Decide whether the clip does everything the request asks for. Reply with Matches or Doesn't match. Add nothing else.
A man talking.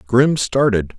Matches